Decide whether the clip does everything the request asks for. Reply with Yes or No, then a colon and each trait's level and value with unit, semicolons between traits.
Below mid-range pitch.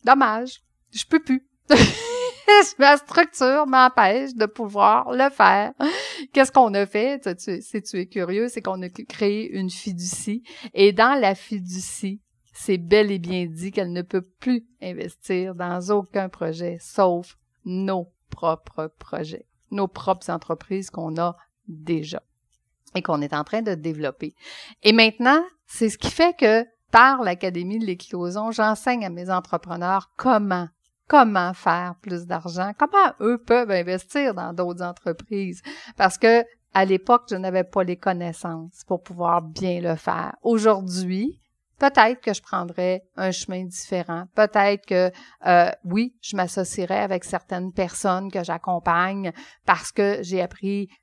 No: high, 190 Hz